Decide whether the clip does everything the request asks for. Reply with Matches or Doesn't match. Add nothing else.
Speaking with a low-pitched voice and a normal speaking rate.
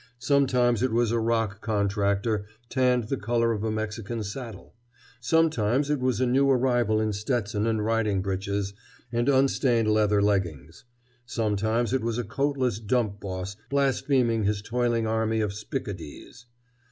Matches